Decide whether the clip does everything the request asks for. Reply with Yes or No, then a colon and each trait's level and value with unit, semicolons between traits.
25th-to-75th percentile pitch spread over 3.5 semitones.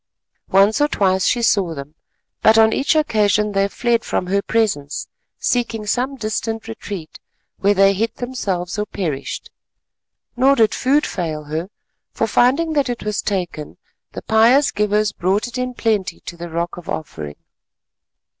Yes: average, 4.4 semitones